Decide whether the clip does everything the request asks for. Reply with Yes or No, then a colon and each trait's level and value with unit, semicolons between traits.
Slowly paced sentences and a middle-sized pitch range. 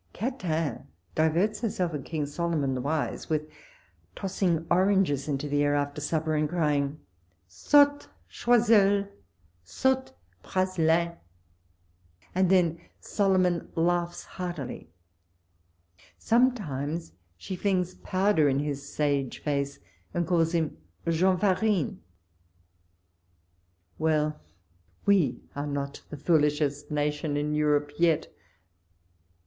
Yes: slow, 105 wpm; average, 4.2 semitones